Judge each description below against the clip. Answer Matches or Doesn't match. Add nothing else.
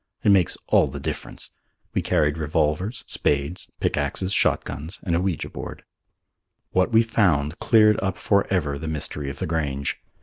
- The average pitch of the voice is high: Doesn't match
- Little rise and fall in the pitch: Doesn't match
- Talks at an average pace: Matches